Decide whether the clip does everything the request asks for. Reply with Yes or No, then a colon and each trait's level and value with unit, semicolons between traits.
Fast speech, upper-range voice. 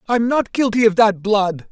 Yes: fast, 210 wpm; high, 215 Hz